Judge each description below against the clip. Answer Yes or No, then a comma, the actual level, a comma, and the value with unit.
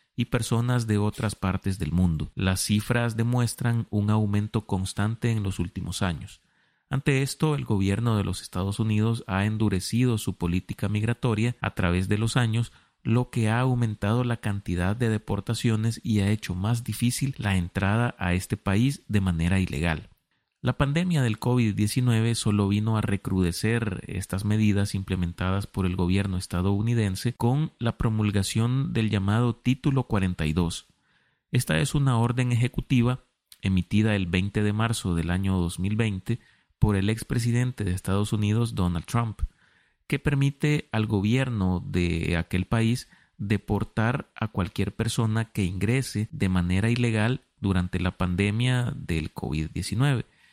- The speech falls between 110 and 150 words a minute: Yes, average, 145 wpm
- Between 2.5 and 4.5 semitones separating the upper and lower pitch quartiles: Yes, average, 3.9 semitones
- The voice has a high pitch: No, low, 105 Hz